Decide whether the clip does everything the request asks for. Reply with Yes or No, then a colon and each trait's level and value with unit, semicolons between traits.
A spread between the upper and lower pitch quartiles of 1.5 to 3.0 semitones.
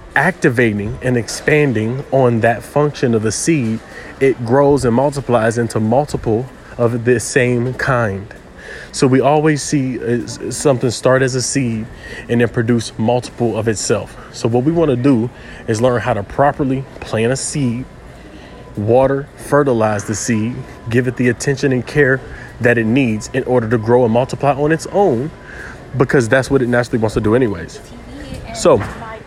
Yes: average, 2.7 semitones